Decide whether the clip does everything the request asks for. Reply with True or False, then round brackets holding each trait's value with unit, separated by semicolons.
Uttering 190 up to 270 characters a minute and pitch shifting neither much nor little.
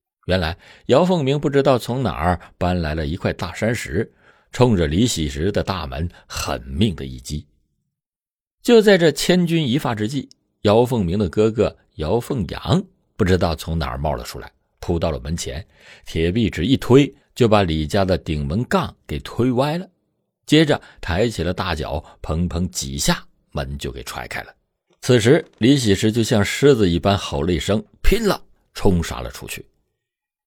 False (240 characters per minute; 7.3 semitones)